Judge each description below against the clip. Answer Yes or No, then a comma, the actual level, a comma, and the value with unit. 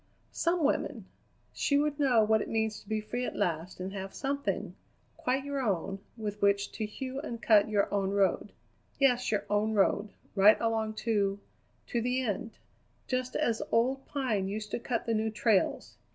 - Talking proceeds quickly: No, average, 180 wpm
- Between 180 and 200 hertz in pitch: No, high, 220 Hz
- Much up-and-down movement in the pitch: No, average, 3.7 semitones